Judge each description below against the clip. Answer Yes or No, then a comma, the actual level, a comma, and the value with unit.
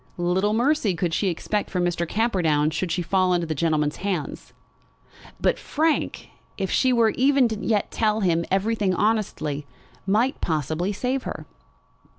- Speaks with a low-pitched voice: No, high, 190 Hz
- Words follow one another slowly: No, average, 150 wpm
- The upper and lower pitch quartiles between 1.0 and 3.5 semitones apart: No, average, 4.7 semitones